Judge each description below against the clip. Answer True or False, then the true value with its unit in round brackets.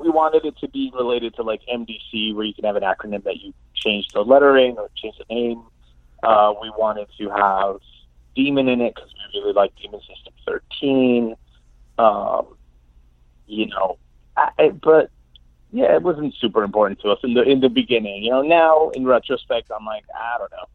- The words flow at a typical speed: True (195 wpm)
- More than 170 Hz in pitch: False (110 Hz)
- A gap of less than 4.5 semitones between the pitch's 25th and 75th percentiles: False (5.4 semitones)